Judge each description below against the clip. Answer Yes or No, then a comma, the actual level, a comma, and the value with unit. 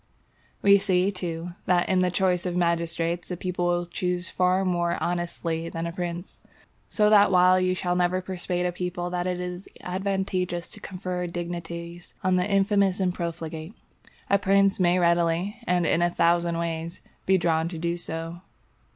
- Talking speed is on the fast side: No, average, 170 wpm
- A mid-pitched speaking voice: Yes, medium, 180 Hz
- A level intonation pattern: Yes, narrow, 1.3 semitones